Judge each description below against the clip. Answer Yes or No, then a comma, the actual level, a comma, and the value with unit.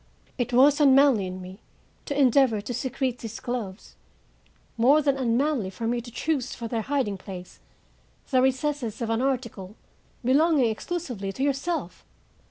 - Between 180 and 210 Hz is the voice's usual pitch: No, very high, 250 Hz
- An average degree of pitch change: Yes, average, 3.8 semitones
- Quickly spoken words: No, average, 150 wpm